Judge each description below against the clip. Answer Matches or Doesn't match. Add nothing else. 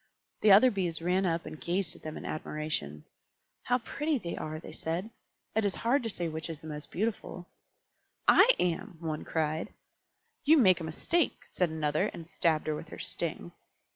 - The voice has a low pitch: Doesn't match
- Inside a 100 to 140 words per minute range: Doesn't match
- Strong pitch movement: Doesn't match